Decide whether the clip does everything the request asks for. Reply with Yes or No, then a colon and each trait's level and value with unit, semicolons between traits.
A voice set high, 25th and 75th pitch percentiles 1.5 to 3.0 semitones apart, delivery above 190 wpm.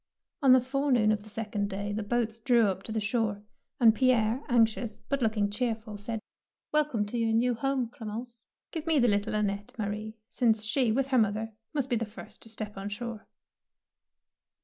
Yes: high, 225 Hz; narrow, 2.6 semitones; fast, 205 wpm